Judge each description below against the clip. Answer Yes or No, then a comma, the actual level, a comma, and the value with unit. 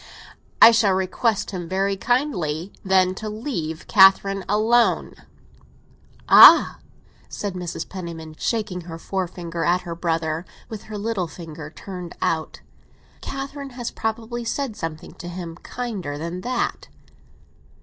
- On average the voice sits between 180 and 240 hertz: Yes, high, 190 Hz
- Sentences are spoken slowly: Yes, slow, 125 wpm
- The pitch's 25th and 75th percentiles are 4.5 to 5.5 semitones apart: Yes, average, 4.8 semitones